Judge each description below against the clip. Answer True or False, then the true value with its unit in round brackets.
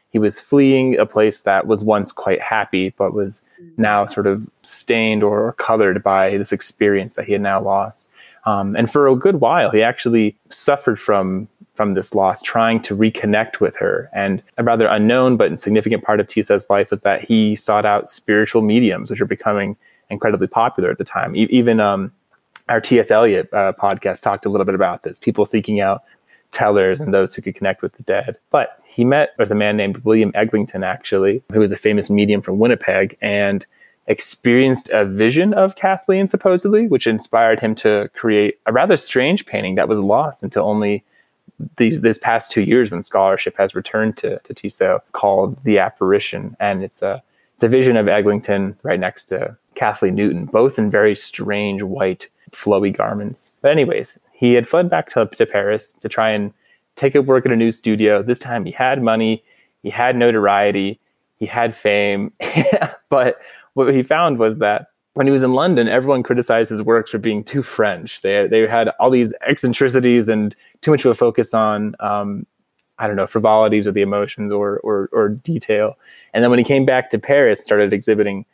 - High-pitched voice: False (110 Hz)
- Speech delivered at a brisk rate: False (195 wpm)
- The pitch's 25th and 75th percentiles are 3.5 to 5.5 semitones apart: False (3.0 semitones)